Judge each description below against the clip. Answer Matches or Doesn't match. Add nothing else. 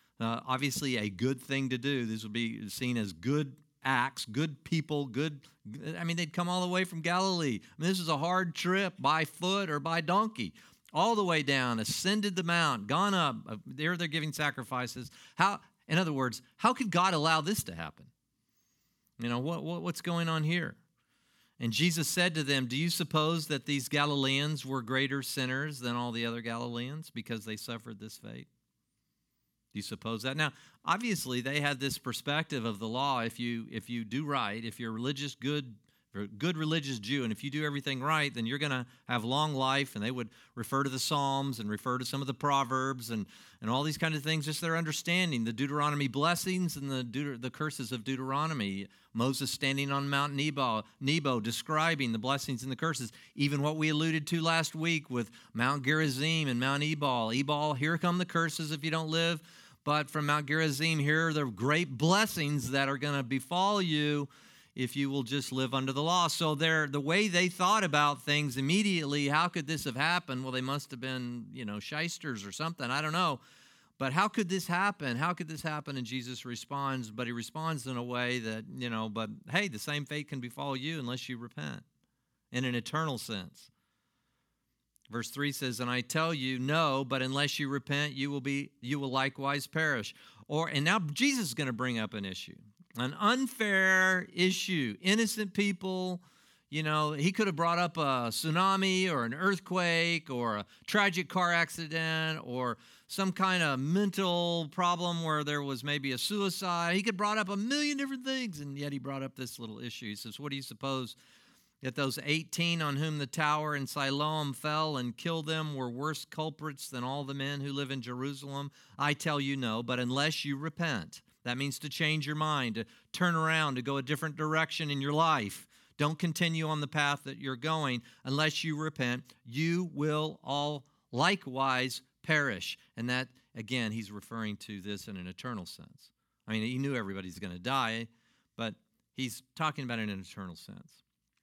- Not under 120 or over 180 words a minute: Doesn't match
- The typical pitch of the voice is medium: Matches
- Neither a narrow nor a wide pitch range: Matches